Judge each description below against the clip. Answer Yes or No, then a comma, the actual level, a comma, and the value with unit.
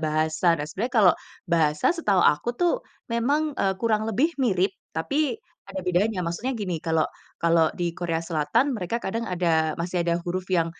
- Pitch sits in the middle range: Yes, medium, 180 Hz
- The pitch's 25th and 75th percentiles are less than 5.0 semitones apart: No, wide, 5.4 semitones